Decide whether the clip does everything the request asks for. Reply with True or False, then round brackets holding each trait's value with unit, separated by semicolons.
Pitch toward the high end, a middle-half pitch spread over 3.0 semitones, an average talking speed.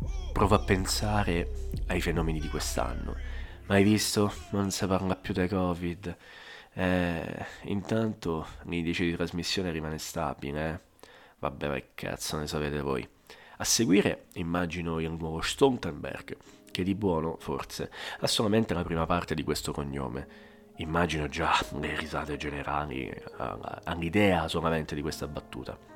False (80 Hz; 3.4 semitones; 130 wpm)